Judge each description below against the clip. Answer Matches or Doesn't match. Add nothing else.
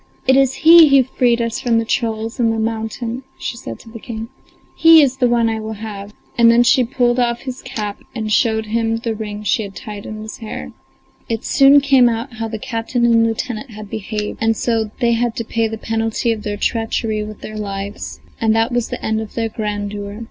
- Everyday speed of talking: Doesn't match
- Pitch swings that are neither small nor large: Doesn't match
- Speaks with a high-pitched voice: Matches